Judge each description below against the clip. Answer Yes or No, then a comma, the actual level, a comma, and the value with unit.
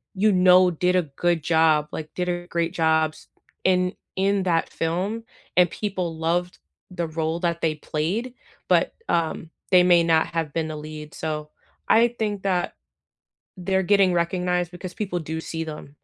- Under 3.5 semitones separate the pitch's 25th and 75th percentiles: Yes, narrow, 2.4 semitones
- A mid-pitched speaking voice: Yes, medium, 175 Hz